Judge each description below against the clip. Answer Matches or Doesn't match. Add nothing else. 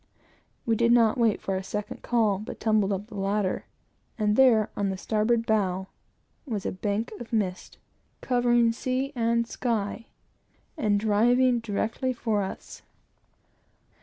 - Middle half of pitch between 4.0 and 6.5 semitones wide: Doesn't match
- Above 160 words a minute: Doesn't match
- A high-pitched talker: Matches